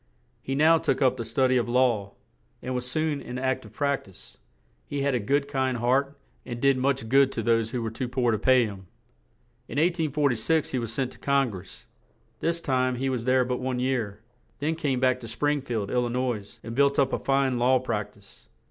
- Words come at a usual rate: No, fast, 220 wpm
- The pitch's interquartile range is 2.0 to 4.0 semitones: Yes, average, 2.7 semitones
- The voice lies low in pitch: Yes, low, 130 Hz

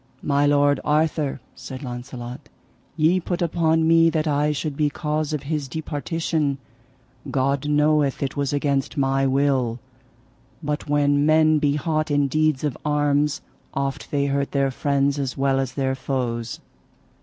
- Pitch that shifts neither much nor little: No, narrow, 2.0 semitones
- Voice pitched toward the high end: No, medium, 145 Hz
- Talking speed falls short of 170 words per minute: Yes, average, 150 wpm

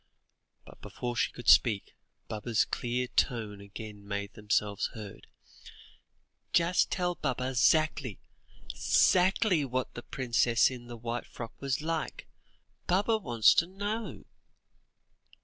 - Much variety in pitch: Yes, wide, 6.8 semitones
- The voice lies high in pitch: No, low, 125 Hz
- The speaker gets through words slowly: Yes, slow, 115 wpm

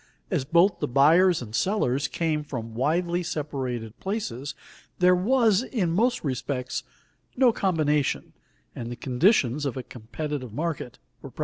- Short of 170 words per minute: Yes, average, 140 wpm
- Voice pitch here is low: No, medium, 150 Hz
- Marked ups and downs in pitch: Yes, wide, 6.2 semitones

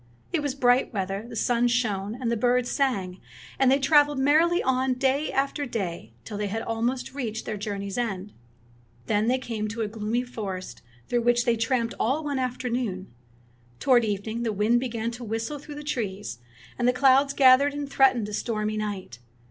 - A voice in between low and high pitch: No, high, 240 Hz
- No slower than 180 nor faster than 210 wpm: Yes, average, 185 wpm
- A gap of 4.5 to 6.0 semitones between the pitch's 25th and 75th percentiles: No, average, 3.7 semitones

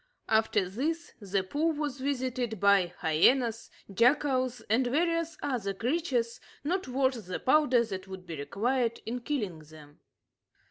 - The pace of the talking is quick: No, slow, 135 wpm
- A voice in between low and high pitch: No, high, 245 Hz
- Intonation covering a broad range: Yes, wide, 5.9 semitones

